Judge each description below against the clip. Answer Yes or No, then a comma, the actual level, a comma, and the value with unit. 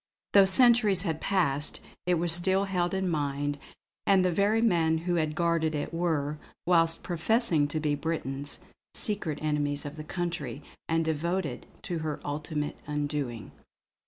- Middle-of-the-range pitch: Yes, medium, 165 Hz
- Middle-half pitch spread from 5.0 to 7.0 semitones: No, average, 3.4 semitones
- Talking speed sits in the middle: Yes, average, 150 wpm